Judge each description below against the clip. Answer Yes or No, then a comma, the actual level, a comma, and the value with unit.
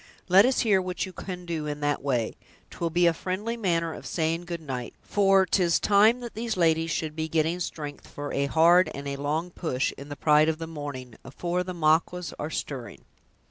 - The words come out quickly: Yes, fast, 210 wpm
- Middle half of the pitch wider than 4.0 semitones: No, average, 3.5 semitones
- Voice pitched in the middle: Yes, medium, 165 Hz